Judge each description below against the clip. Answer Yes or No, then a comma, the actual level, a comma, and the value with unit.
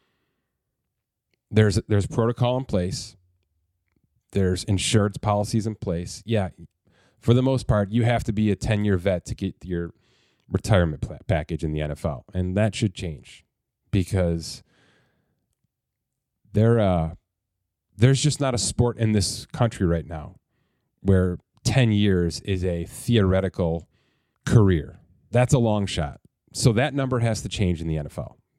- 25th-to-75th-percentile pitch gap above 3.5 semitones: Yes, average, 4.5 semitones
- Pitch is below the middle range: Yes, low, 100 Hz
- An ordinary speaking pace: Yes, average, 145 wpm